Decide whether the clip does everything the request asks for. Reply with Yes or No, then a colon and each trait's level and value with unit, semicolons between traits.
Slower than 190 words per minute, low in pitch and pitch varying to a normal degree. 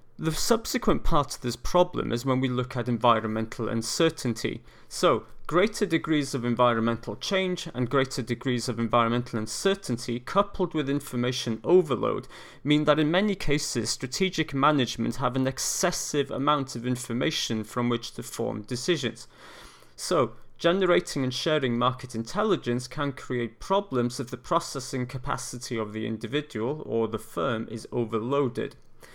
Yes: average, 140 wpm; low, 125 Hz; average, 4.3 semitones